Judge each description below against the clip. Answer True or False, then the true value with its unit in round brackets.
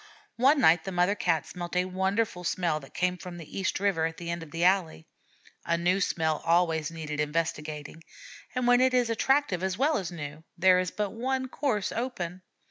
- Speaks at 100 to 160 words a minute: False (200 wpm)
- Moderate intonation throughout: True (4.0 semitones)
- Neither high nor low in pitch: True (180 Hz)